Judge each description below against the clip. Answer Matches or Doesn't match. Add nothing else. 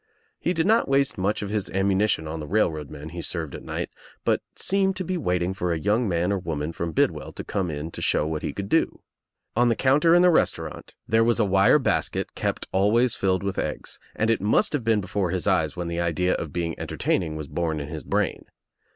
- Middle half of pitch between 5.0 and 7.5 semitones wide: Matches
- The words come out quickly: Matches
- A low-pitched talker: Matches